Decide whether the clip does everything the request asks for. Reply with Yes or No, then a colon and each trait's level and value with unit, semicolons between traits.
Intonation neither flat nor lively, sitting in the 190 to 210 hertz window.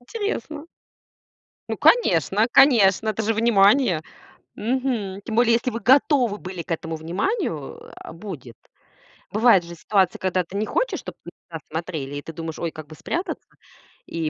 No: wide, 6.5 semitones; high, 200 Hz